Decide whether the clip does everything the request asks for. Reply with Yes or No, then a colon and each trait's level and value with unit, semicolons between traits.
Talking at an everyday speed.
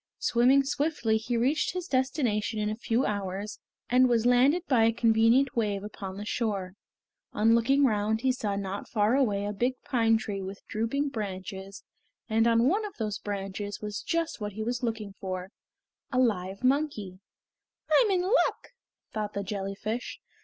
Yes: average, 165 wpm